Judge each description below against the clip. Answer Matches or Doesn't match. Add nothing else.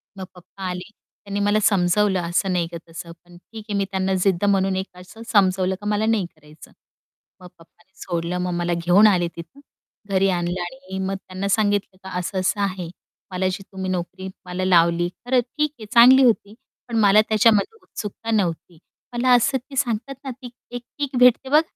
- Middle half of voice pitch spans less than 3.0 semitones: Doesn't match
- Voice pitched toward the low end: Doesn't match